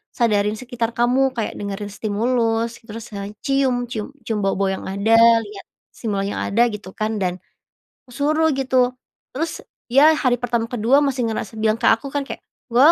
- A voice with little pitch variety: No, average, 3.5 semitones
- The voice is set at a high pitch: Yes, high, 230 Hz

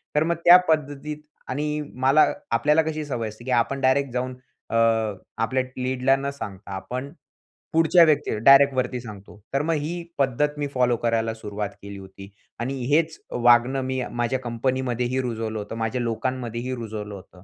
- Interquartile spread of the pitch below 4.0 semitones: Yes, average, 3.5 semitones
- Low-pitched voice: Yes, low, 130 Hz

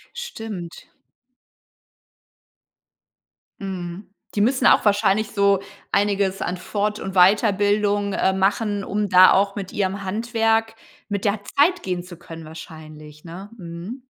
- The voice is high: Yes, high, 200 Hz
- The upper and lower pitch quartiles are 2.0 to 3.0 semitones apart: Yes, narrow, 2.5 semitones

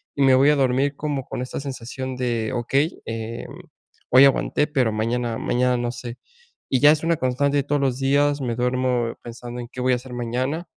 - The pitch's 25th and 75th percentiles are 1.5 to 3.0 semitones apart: Yes, narrow, 2.5 semitones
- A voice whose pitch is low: Yes, low, 130 Hz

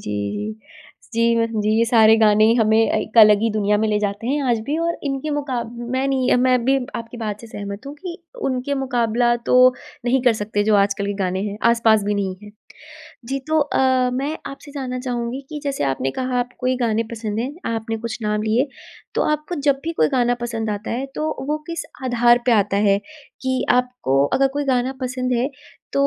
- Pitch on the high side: Yes, high, 240 Hz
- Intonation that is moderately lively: Yes, average, 3.4 semitones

